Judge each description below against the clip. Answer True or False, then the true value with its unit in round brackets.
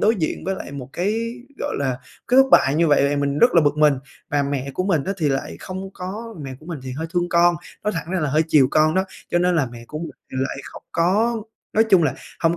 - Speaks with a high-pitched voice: False (165 Hz)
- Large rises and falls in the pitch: False (4.8 semitones)